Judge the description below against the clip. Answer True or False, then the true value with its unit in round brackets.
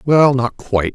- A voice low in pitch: True (125 Hz)